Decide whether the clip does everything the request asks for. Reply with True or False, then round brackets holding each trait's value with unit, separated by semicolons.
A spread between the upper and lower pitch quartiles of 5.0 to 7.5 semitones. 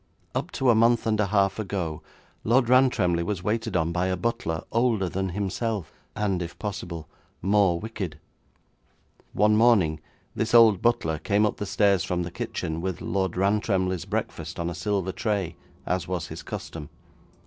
False (3.6 semitones)